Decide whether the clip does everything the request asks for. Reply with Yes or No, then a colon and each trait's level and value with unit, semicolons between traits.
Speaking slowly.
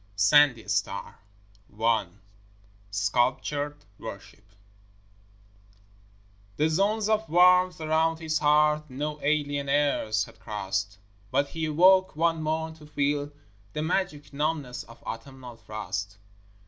Yes: slow, 110 wpm